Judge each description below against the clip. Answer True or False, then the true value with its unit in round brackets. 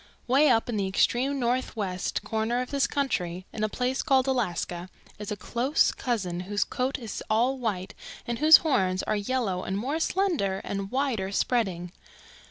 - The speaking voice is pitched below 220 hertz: False (230 Hz)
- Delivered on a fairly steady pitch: False (5.3 semitones)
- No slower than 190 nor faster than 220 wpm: False (170 wpm)